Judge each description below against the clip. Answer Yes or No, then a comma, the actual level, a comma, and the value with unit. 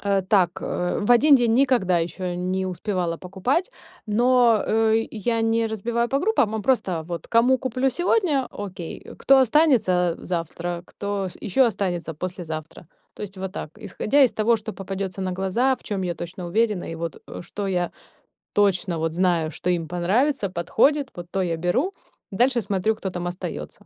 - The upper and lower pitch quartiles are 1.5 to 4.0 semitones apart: No, average, 4.9 semitones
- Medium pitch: No, high, 195 Hz